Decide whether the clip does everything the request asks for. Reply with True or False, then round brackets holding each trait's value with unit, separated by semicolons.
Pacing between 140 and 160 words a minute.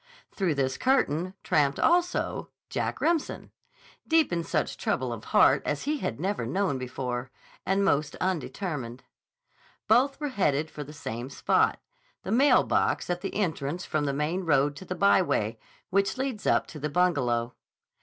True (155 wpm)